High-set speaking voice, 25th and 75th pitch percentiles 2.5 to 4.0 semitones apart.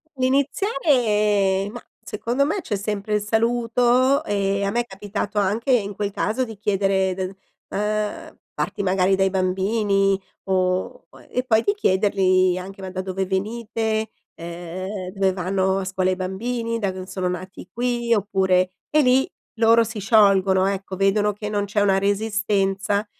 Yes: high, 200 Hz; average, 2.8 semitones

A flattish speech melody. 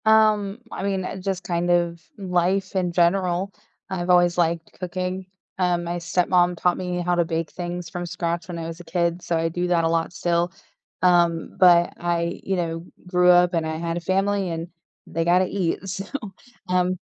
Yes: narrow, 1.3 semitones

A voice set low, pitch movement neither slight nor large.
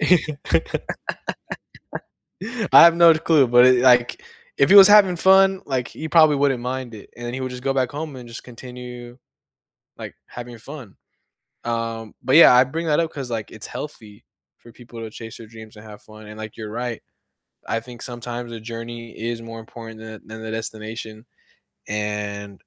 Yes: low, 120 Hz; average, 3.1 semitones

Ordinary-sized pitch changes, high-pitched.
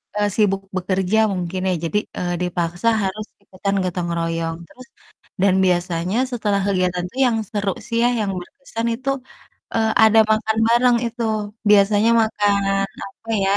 Yes: average, 3.4 semitones; high, 200 Hz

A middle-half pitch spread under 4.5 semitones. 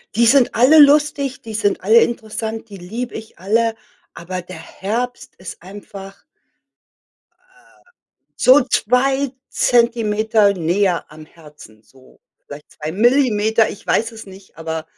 No: average, 4.9 semitones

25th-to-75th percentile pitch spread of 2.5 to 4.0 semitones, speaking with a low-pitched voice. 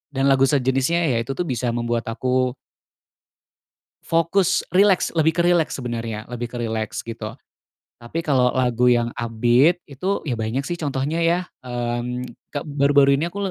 No: average, 5.2 semitones; low, 130 Hz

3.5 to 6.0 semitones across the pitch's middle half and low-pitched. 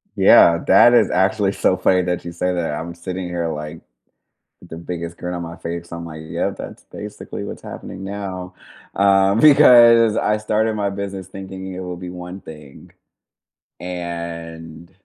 No: narrow, 2.5 semitones; very low, 90 Hz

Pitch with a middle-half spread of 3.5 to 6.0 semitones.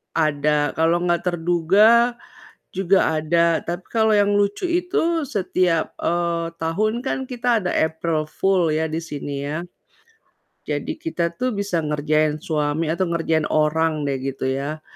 Yes: average, 4.5 semitones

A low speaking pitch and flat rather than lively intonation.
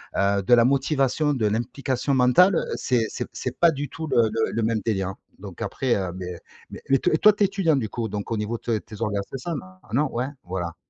No: low, 120 Hz; average, 4.7 semitones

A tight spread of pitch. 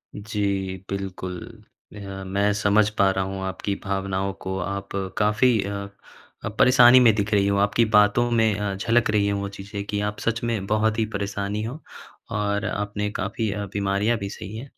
Yes: narrow, 1.6 semitones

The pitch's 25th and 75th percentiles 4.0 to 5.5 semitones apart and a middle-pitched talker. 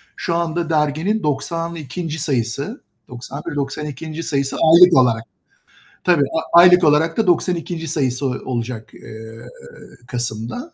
Yes: average, 4.7 semitones; medium, 150 Hz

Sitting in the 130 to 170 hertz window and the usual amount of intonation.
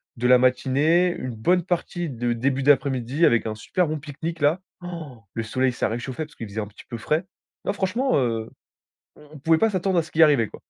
No: medium, 140 Hz; wide, 5.7 semitones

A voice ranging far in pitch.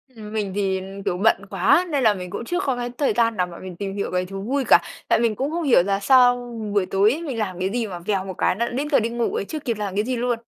No: average, 4.1 semitones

